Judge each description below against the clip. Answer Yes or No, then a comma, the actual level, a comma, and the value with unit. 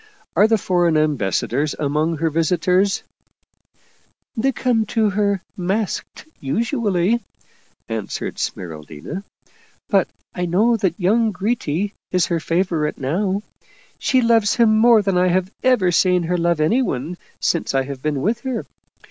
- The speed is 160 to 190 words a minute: No, average, 150 wpm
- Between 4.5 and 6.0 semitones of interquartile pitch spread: Yes, wide, 5.6 semitones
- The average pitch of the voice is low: No, medium, 180 Hz